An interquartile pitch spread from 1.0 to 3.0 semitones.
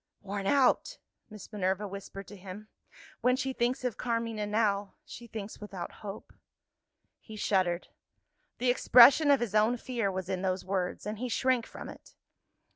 No: average, 3.7 semitones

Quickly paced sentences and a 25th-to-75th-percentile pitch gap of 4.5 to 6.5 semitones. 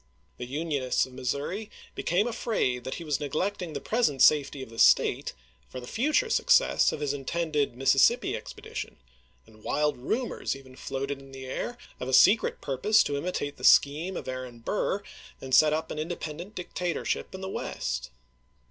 No: average, 180 wpm; wide, 5.6 semitones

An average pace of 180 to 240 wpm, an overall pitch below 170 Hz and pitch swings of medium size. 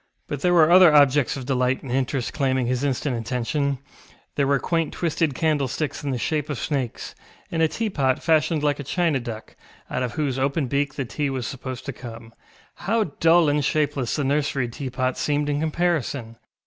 Yes: average, 185 wpm; medium, 140 Hz; average, 3.1 semitones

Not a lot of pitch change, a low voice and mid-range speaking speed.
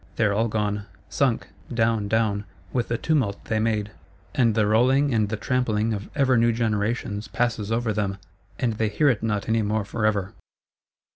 Yes: narrow, 2.1 semitones; low, 110 Hz; average, 170 wpm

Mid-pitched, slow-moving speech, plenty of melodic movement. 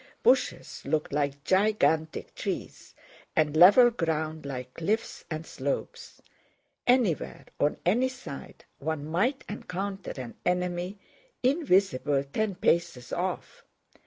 Yes: medium, 175 Hz; slow, 105 wpm; wide, 5.8 semitones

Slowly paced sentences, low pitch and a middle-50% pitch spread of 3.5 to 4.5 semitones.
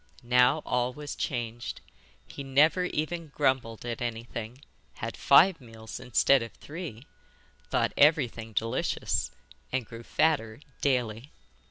Yes: slow, 120 wpm; low, 125 Hz; average, 4.2 semitones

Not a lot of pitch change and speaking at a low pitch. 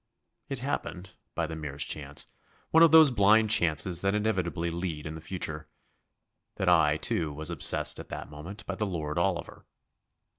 No: average, 4.8 semitones; very low, 85 Hz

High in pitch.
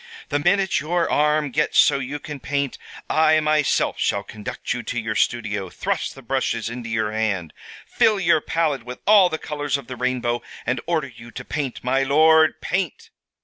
No: low, 135 Hz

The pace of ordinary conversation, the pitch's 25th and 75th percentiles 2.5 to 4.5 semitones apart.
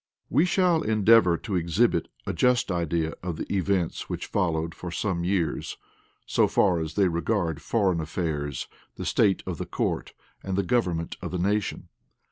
Yes: average, 165 wpm; average, 3.6 semitones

